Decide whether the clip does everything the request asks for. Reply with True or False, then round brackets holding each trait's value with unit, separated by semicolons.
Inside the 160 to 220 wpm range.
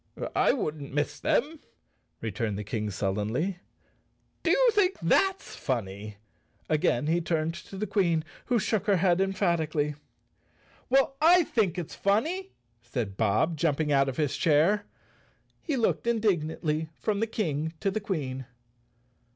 False (140 wpm)